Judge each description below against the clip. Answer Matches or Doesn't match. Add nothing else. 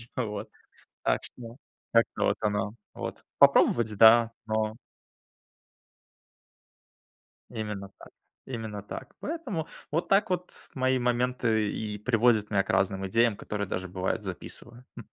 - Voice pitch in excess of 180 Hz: Doesn't match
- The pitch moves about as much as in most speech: Matches